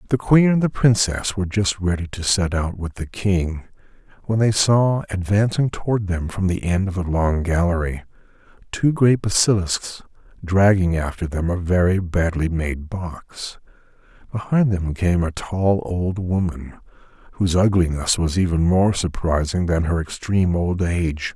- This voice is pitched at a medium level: No, very low, 90 Hz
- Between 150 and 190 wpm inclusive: Yes, average, 155 wpm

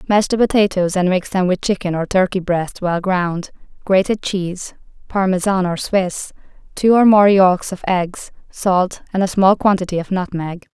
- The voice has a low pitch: No, medium, 185 Hz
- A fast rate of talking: No, average, 175 wpm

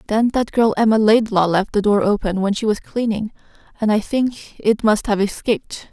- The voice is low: No, high, 215 Hz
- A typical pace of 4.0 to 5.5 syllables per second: Yes, 5.0 syllables/s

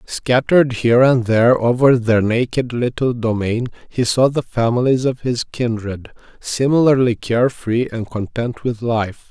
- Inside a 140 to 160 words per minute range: Yes, average, 150 wpm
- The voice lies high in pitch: No, low, 120 Hz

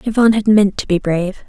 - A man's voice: No, female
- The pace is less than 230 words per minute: No, fast, 245 wpm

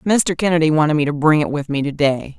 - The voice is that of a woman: Yes, female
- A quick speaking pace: Yes, fast, 275 wpm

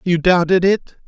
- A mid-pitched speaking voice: Yes, medium, 180 Hz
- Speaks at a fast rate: No, average, 165 wpm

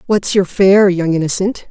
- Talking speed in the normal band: Yes, average, 175 wpm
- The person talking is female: Yes, female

